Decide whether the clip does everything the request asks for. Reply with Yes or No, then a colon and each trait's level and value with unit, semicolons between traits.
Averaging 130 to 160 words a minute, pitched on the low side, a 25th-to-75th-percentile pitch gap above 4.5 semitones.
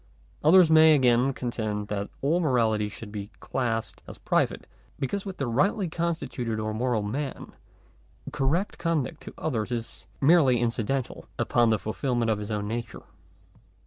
Yes: average, 150 wpm; low, 125 Hz; wide, 5.6 semitones